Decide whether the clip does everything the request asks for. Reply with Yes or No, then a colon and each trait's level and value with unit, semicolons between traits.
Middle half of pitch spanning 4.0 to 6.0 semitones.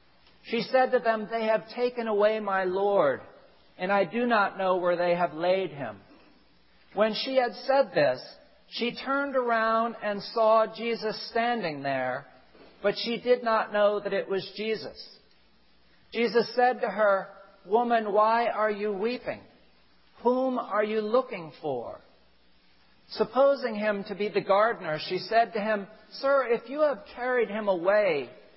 No: average, 3.3 semitones